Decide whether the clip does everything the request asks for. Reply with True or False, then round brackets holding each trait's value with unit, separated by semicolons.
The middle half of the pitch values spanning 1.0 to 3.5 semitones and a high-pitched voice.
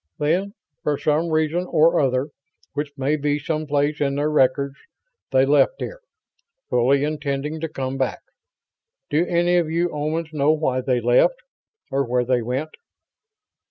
False (2.7 semitones; 150 Hz)